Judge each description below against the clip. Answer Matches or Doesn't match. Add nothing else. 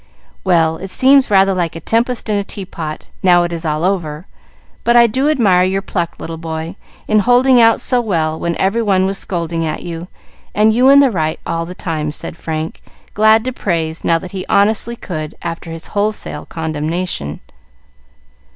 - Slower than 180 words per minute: Doesn't match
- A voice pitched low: Doesn't match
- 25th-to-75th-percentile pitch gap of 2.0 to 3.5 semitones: Doesn't match